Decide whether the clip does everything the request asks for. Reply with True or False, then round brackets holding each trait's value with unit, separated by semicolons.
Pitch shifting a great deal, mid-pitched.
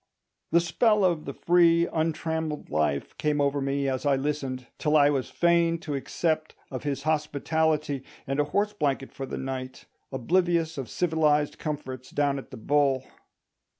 False (2.9 semitones; 150 Hz)